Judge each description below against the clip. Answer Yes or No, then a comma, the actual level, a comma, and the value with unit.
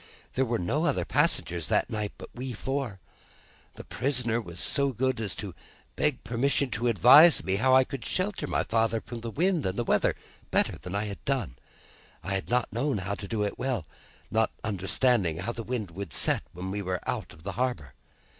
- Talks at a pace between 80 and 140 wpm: No, average, 200 wpm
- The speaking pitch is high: No, low, 115 Hz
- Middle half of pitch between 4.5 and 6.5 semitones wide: Yes, average, 4.8 semitones